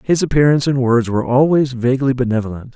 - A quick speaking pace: No, average, 175 wpm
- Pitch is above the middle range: No, low, 130 Hz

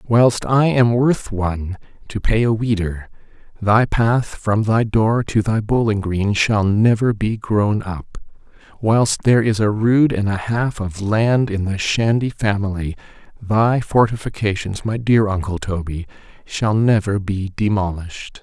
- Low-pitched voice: Yes, low, 105 Hz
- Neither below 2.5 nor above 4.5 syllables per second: Yes, 4.0 syllables/s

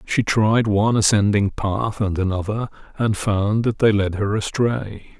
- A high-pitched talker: No, low, 105 Hz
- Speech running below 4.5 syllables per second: Yes, 4.3 syllables/s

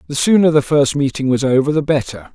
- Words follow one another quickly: Yes, fast, 230 wpm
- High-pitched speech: No, medium, 140 Hz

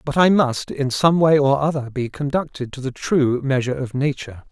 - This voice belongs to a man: Yes, male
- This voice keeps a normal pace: No, fast, 215 wpm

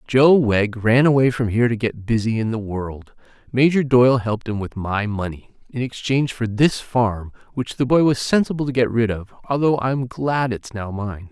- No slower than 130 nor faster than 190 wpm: No, average, 200 wpm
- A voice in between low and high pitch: No, low, 120 Hz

